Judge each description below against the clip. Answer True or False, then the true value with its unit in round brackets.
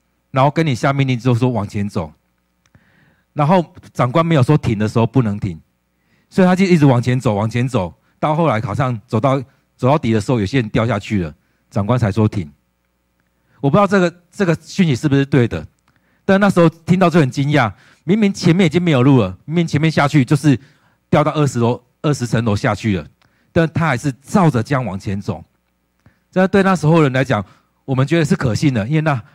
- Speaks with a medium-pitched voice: False (130 Hz)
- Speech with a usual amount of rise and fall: False (6.9 semitones)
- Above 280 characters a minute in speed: True (305 characters per minute)